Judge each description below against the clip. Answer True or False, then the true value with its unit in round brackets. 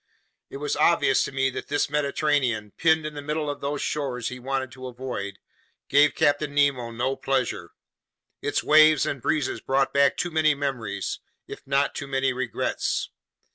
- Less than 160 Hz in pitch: True (140 Hz)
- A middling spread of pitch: False (2.3 semitones)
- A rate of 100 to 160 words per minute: False (170 wpm)